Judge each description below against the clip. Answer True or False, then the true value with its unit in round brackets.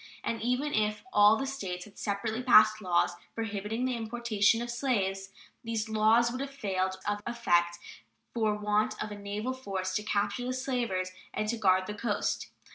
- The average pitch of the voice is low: False (215 Hz)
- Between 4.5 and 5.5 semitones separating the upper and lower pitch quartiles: False (2.8 semitones)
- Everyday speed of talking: True (175 wpm)